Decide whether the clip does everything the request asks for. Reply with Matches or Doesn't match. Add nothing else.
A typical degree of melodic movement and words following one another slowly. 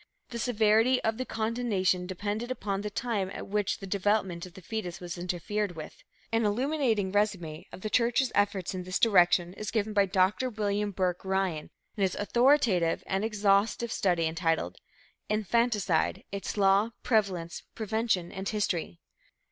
Doesn't match